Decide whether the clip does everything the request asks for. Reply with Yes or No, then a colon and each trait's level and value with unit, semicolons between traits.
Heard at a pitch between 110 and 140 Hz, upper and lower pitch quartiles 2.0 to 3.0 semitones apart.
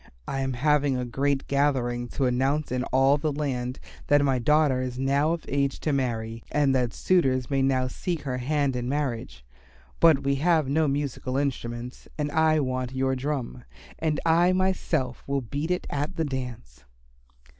Yes: low, 135 Hz; average, 2.7 semitones